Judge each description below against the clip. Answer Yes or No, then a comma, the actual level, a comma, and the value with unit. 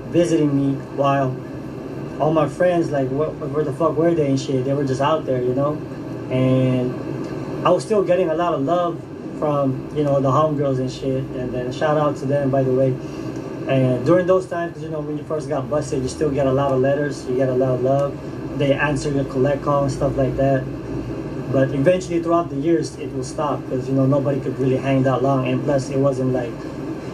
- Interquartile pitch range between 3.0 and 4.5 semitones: No, narrow, 2.4 semitones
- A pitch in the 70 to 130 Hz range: No, medium, 140 Hz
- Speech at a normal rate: No, fast, 225 wpm